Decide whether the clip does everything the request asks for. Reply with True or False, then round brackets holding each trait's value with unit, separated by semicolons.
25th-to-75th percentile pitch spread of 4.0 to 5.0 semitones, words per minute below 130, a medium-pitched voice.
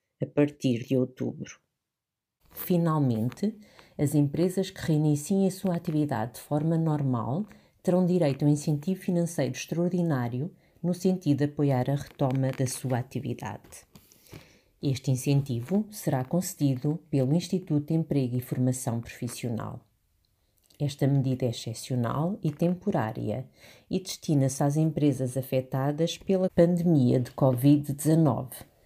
True (4.7 semitones; 120 wpm; 145 Hz)